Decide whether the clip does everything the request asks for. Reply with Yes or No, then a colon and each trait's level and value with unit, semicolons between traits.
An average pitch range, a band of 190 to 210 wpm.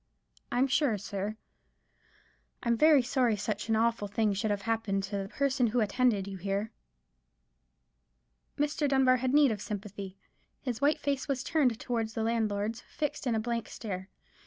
No: average, 4.0 semitones; average, 160 wpm